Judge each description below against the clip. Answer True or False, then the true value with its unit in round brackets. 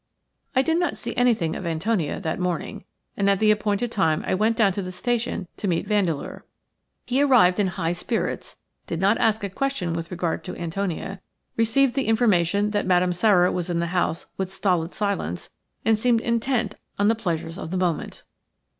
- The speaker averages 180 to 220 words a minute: True (190 wpm)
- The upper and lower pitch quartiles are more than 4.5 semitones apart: False (4.2 semitones)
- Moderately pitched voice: False (195 Hz)